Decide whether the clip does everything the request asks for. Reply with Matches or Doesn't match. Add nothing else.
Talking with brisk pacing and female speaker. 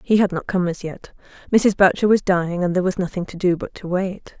Matches